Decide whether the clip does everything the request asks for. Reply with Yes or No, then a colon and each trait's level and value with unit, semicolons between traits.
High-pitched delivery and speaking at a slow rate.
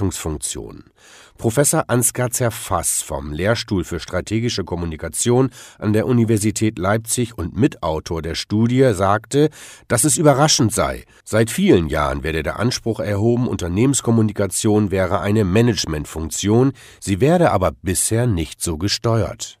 No: low, 110 Hz; slow, 120 wpm